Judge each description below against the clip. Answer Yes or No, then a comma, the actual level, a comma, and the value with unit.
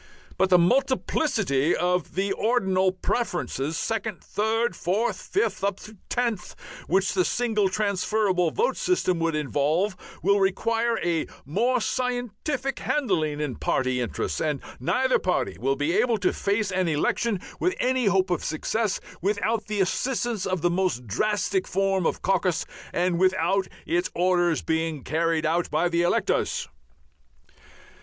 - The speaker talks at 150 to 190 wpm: No, average, 140 wpm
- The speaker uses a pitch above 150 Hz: Yes, high, 190 Hz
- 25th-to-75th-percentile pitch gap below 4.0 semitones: No, average, 4.7 semitones